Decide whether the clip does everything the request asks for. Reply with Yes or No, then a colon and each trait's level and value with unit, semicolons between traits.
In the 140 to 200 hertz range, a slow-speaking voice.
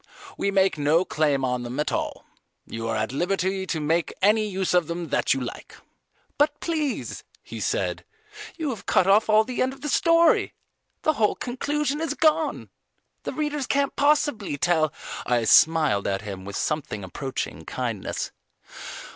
No: high, 190 Hz; average, 170 wpm